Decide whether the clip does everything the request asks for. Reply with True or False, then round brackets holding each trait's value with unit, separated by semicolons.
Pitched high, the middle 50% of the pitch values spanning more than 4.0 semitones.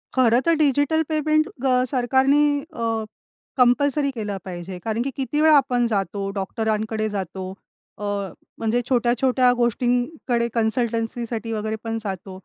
False (240 Hz; 3.5 semitones)